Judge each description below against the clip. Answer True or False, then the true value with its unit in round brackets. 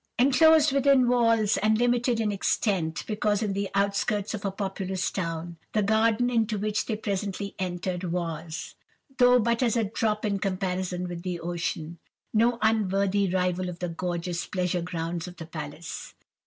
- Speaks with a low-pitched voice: False (195 Hz)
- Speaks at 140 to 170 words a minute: True (155 wpm)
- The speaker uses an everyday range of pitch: True (3.7 semitones)